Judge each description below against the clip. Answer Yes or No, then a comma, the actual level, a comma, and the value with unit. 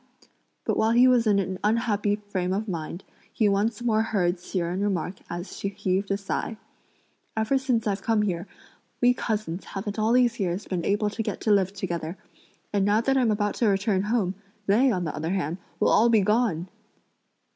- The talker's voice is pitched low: No, high, 205 Hz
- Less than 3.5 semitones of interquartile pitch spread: Yes, average, 3.0 semitones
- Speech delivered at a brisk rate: No, average, 195 wpm